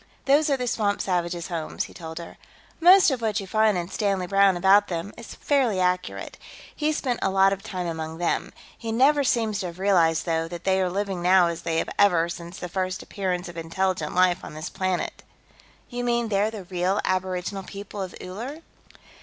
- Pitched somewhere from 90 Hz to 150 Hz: No, high, 190 Hz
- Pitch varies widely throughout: No, average, 3.3 semitones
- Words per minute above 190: Yes, fast, 205 wpm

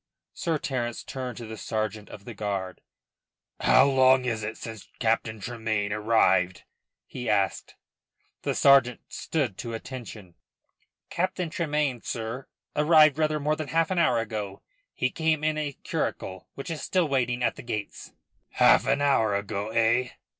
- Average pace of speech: Yes, average, 155 wpm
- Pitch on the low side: Yes, low, 120 Hz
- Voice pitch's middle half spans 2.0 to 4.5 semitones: No, average, 5.0 semitones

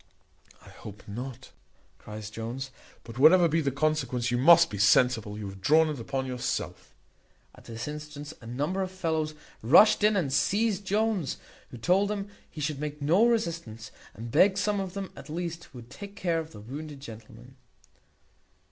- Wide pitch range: Yes, wide, 6.7 semitones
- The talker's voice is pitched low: No, medium, 150 Hz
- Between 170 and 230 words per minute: Yes, average, 175 wpm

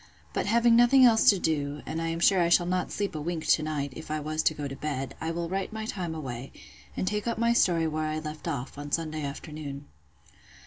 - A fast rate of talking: Yes, fast, 240 wpm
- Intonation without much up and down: No, average, 3.8 semitones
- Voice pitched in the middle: Yes, medium, 160 Hz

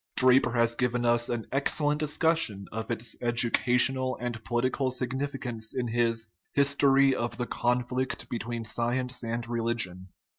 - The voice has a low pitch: Yes, low, 120 Hz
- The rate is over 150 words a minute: No, average, 140 wpm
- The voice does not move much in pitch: Yes, narrow, 1.8 semitones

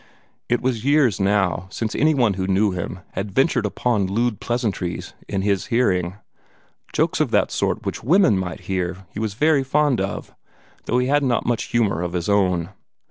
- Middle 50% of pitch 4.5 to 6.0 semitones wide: Yes, average, 4.8 semitones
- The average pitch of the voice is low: Yes, low, 105 Hz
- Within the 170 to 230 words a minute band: Yes, average, 185 wpm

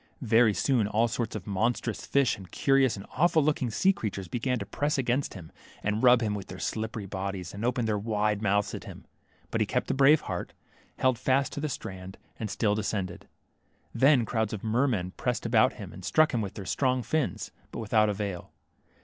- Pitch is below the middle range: Yes, low, 110 Hz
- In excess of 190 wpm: Yes, fast, 205 wpm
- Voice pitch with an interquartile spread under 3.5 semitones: No, average, 4.0 semitones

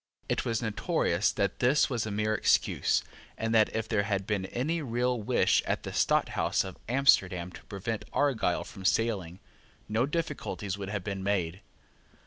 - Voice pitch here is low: Yes, low, 110 Hz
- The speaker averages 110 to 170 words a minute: Yes, average, 165 wpm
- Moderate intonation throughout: Yes, average, 3.7 semitones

